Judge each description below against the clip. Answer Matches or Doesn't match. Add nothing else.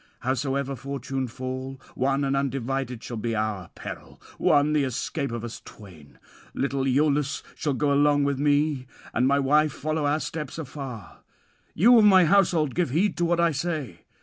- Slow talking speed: Doesn't match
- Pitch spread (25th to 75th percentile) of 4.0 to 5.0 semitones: Doesn't match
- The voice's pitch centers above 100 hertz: Matches